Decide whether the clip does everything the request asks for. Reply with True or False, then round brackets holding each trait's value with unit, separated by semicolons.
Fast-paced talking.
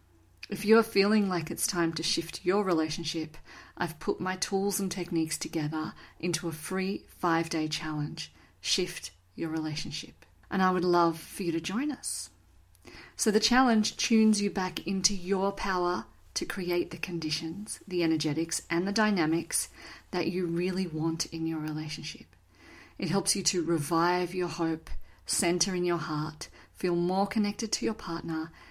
False (160 wpm)